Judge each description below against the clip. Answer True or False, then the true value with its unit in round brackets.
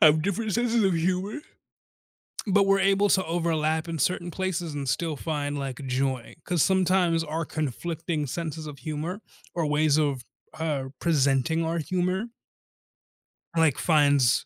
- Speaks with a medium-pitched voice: True (160 Hz)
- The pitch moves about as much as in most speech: True (3.7 semitones)